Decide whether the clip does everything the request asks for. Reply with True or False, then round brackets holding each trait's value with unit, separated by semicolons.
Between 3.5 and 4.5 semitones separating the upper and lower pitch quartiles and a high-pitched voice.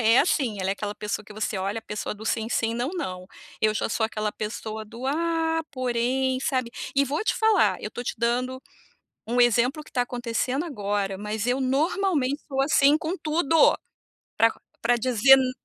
True (4.2 semitones; 245 Hz)